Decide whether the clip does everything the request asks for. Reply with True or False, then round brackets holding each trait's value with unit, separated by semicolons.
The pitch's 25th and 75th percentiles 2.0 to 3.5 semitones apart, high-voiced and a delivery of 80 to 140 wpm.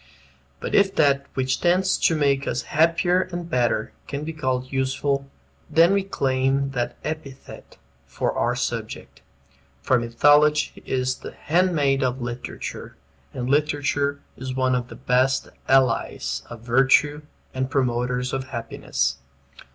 False (2.8 semitones; 135 Hz; 135 wpm)